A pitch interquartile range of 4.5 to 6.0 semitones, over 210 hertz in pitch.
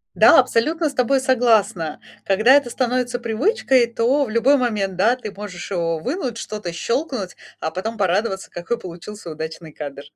Yes: wide, 5.6 semitones; high, 225 Hz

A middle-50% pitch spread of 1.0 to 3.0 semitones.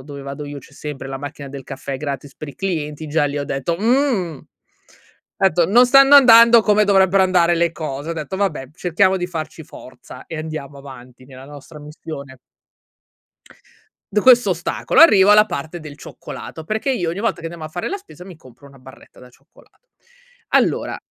No: average, 5.3 semitones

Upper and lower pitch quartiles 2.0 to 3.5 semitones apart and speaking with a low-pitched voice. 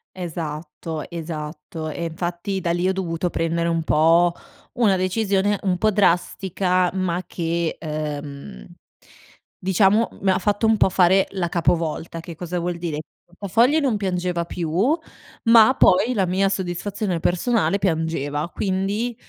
No: average, 2.8 semitones; medium, 180 Hz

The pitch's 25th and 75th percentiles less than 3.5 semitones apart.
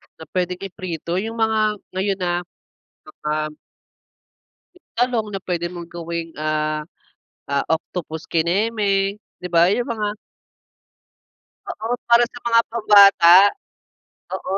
No: average, 4.3 semitones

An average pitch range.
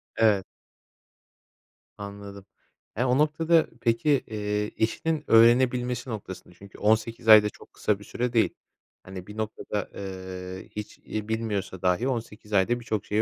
Yes: average, 3.1 semitones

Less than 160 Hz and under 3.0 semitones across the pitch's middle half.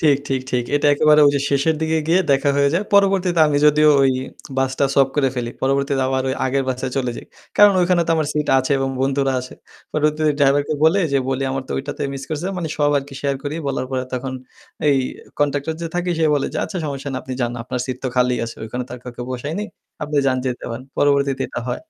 Yes: medium, 140 Hz; narrow, 2.5 semitones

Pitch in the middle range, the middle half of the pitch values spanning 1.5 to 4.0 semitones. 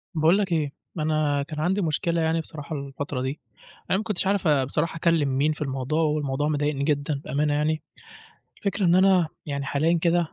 Yes: medium, 155 Hz; average, 2.8 semitones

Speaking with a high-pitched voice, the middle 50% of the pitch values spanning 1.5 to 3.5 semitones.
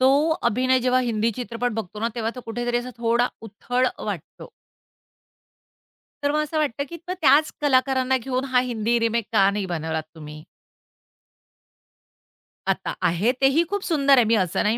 Yes: high, 240 Hz; average, 3.2 semitones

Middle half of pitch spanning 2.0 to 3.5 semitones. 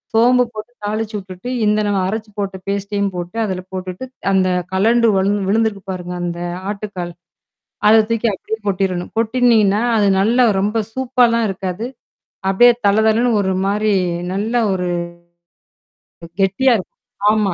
Yes: average, 3.0 semitones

